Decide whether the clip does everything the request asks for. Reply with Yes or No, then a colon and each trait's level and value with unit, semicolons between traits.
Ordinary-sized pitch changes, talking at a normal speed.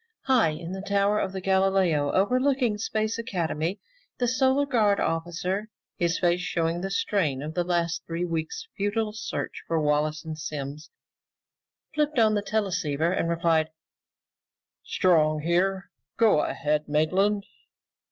No: average, 4.5 semitones; slow, 130 wpm